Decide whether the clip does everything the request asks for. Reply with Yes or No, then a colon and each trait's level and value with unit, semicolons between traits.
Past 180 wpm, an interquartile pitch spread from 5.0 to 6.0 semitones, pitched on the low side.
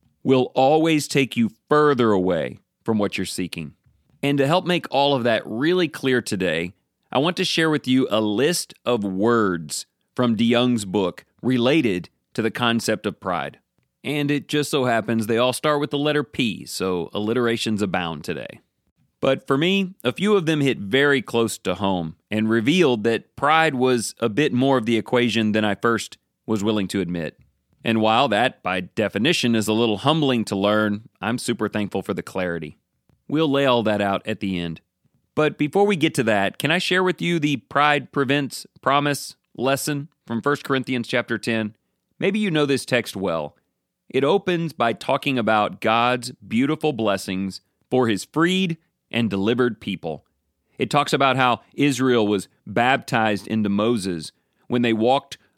No: average, 175 wpm; wide, 5.4 semitones; low, 120 Hz